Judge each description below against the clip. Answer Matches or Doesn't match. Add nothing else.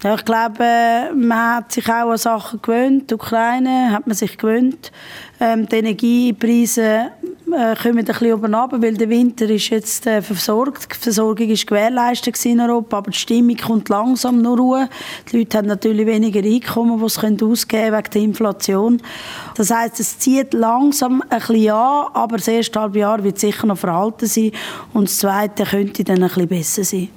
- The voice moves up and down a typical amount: Doesn't match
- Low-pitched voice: Doesn't match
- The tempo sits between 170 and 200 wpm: Matches